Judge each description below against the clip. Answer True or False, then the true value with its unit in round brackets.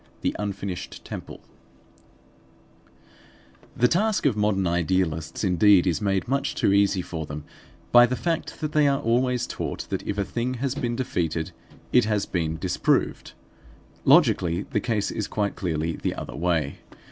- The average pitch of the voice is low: True (100 Hz)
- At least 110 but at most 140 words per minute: False (155 wpm)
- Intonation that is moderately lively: False (6.0 semitones)